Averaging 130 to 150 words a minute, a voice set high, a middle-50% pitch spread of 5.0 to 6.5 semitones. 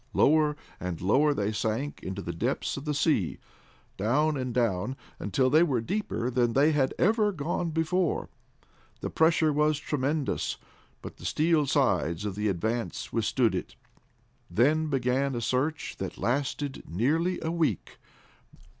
No: average, 145 wpm; low, 135 Hz; wide, 5.4 semitones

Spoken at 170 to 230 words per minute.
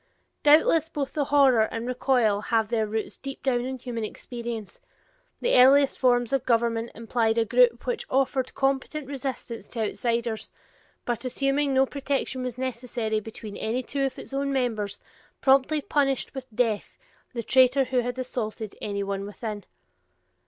No: average, 150 wpm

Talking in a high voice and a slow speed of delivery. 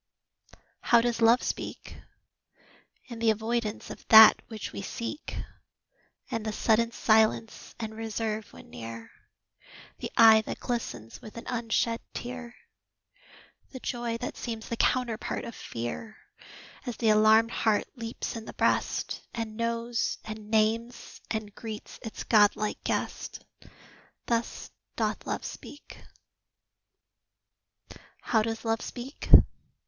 Yes: high, 225 Hz; slow, 120 wpm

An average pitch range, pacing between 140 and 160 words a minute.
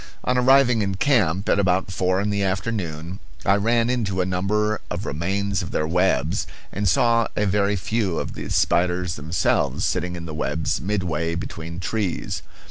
No: average, 3.5 semitones; average, 170 wpm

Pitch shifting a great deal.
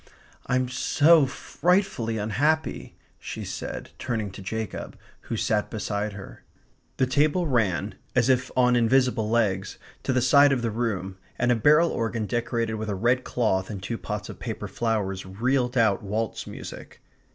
No: average, 3.5 semitones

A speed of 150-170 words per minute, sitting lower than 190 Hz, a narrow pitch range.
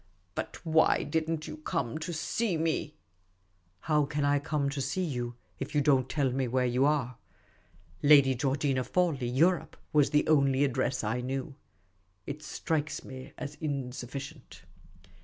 No: average, 165 wpm; medium, 140 Hz; average, 3.3 semitones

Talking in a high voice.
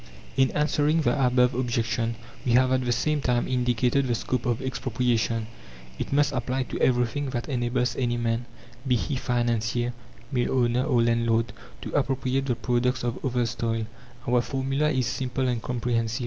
No: low, 125 Hz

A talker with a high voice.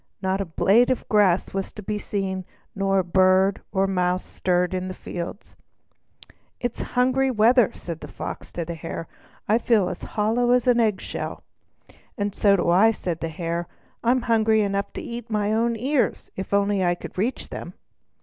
Yes: high, 200 Hz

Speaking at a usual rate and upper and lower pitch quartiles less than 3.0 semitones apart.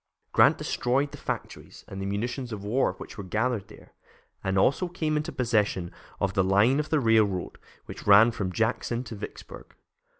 No: average, 170 wpm; average, 4.3 semitones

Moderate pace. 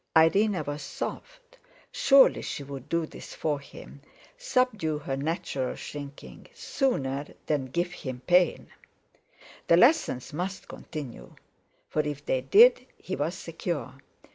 No: slow, 125 wpm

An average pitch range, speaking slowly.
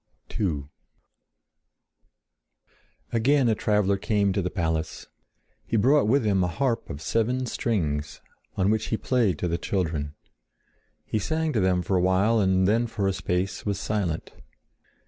No: average, 4.1 semitones; average, 150 wpm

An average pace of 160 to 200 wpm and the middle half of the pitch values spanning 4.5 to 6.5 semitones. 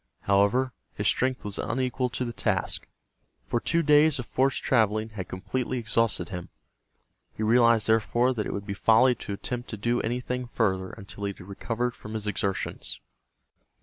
No: average, 170 wpm; average, 3.5 semitones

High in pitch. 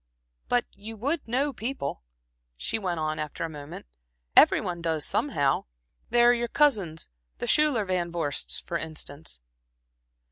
No: medium, 180 Hz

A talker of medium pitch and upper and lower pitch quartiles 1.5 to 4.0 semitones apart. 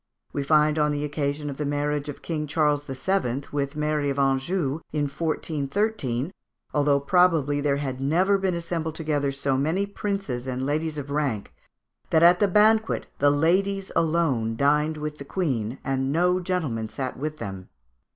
Yes: medium, 150 Hz; average, 3.2 semitones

